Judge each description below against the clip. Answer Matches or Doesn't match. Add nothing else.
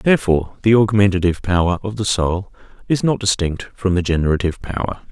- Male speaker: Matches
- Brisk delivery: Doesn't match